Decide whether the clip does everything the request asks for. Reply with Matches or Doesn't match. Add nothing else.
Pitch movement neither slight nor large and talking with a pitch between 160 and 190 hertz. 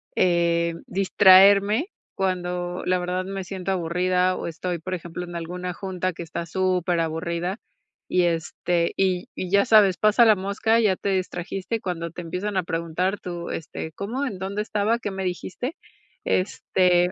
Doesn't match